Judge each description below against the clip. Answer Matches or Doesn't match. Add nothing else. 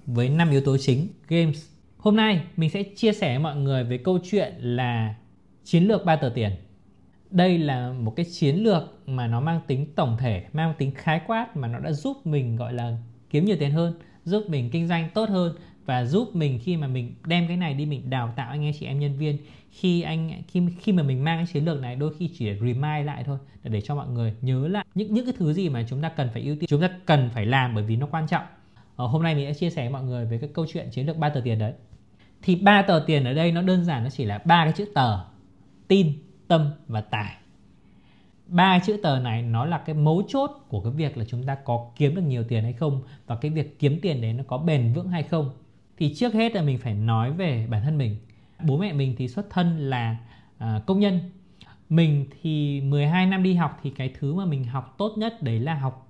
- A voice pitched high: Doesn't match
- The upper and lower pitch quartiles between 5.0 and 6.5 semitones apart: Matches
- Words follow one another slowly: Doesn't match